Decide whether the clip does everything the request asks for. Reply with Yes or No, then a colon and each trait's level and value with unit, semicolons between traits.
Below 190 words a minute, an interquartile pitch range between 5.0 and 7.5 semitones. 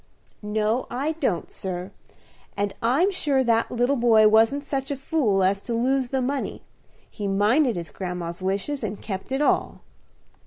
Yes: average, 160 wpm; average, 5.3 semitones